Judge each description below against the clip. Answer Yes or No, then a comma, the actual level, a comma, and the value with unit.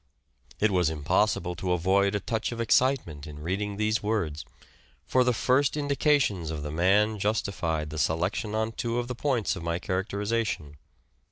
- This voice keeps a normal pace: Yes, average, 165 wpm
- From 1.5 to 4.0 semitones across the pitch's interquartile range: No, average, 5.2 semitones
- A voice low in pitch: Yes, low, 100 Hz